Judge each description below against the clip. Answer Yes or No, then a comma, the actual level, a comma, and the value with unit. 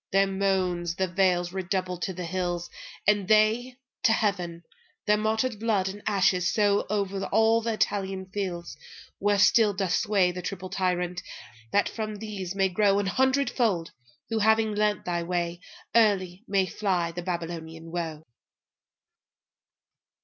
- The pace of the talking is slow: Yes, slow, 125 wpm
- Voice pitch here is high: Yes, high, 195 Hz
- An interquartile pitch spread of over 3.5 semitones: No, average, 2.9 semitones